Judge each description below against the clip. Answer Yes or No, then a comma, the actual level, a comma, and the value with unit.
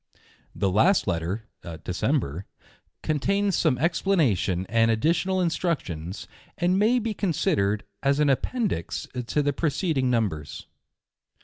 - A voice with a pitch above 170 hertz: No, medium, 140 Hz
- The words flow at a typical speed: No, slow, 115 wpm